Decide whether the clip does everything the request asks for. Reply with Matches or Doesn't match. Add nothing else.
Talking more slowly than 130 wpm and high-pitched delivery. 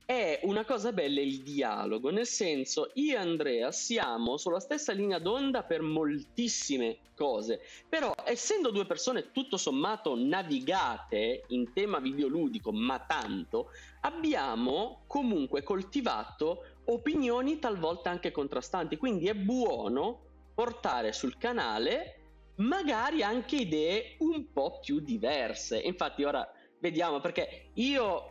Matches